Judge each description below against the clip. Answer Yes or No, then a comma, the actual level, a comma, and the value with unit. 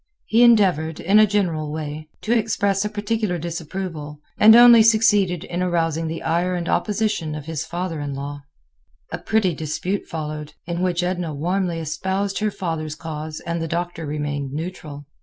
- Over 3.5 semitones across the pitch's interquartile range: Yes, average, 4.0 semitones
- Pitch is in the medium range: Yes, medium, 170 Hz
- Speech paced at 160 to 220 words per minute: Yes, average, 165 wpm